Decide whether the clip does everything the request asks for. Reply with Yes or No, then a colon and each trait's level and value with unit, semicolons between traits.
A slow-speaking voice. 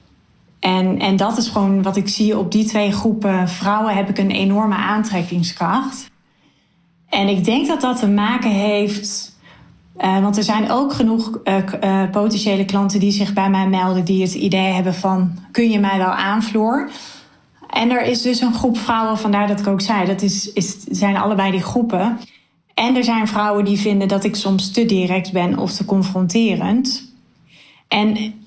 No: average, 180 wpm